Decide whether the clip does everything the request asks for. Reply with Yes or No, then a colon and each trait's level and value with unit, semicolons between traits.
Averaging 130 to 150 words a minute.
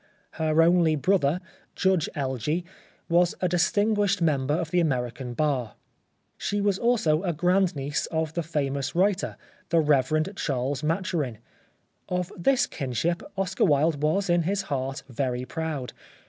Yes: average, 140 wpm